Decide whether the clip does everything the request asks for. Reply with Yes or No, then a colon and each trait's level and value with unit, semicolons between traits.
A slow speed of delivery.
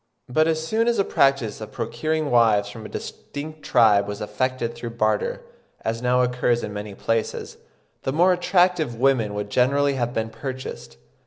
No: average, 170 wpm